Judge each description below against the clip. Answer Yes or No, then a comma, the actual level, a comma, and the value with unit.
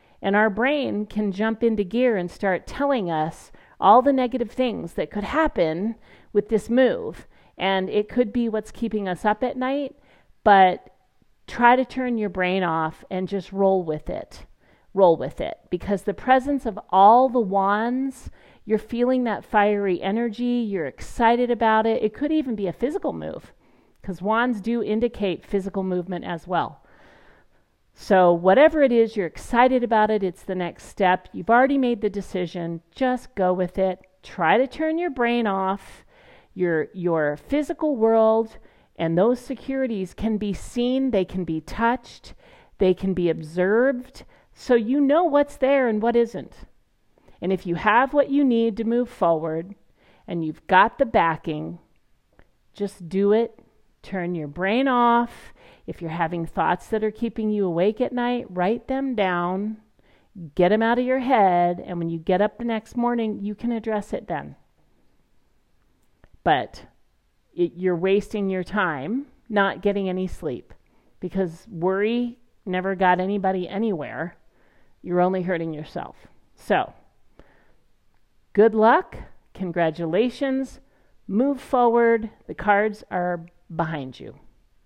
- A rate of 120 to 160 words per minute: Yes, average, 155 wpm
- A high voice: Yes, high, 210 Hz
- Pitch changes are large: No, average, 4.8 semitones